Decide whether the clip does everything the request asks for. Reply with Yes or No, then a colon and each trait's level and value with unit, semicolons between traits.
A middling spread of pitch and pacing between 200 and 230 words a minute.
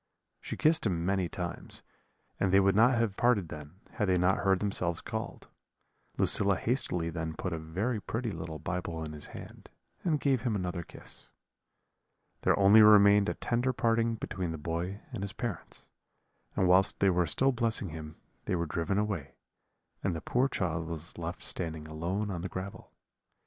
No: average, 4.3 semitones; average, 175 wpm